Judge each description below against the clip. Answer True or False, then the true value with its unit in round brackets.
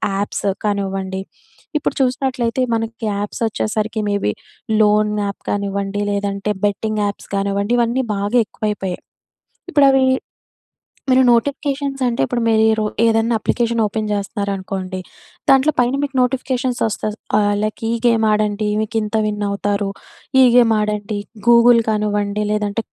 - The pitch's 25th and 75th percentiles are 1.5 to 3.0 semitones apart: True (2.7 semitones)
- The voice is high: True (215 Hz)